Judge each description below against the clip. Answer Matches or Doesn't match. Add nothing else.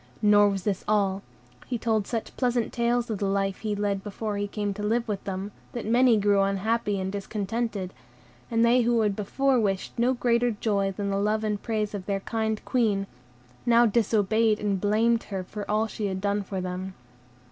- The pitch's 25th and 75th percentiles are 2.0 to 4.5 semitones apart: Matches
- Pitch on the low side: Doesn't match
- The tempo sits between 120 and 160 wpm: Doesn't match